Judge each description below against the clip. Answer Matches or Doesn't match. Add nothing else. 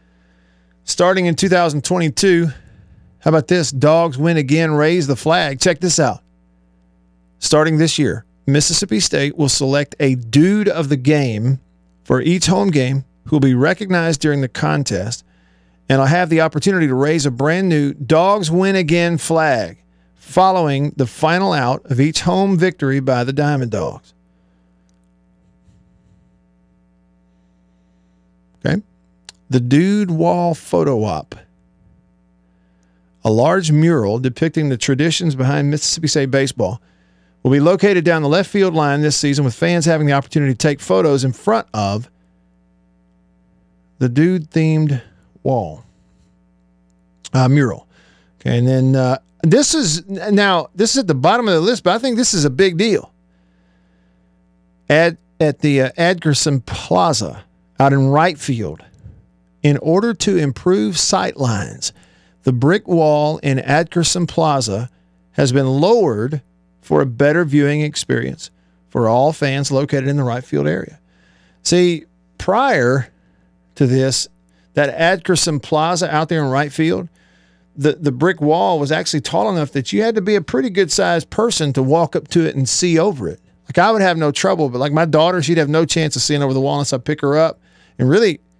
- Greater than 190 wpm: Doesn't match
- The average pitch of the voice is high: Doesn't match